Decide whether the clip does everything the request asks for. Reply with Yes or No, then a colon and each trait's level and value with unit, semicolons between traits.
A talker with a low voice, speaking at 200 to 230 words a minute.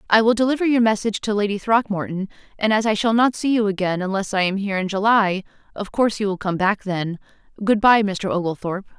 No: high, 205 Hz; fast, 205 wpm